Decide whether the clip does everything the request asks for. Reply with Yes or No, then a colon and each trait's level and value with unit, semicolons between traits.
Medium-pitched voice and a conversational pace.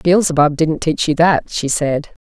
Yes: medium, 155 Hz; average, 190 wpm